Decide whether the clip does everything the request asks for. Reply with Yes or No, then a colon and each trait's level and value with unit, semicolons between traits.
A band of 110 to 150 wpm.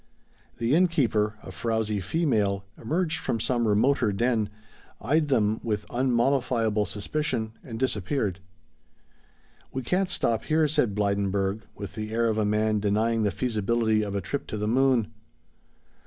Yes: average, 145 wpm